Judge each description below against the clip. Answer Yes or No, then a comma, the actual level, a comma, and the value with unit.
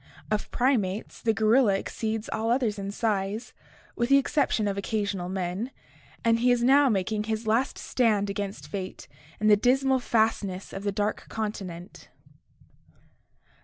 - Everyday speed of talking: Yes, average, 145 wpm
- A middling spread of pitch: Yes, average, 3.1 semitones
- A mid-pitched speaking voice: No, high, 215 Hz